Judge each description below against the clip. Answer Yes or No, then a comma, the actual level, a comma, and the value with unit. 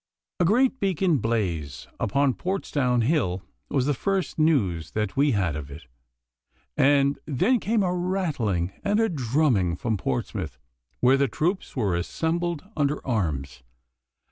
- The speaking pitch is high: No, low, 135 Hz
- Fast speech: No, average, 140 wpm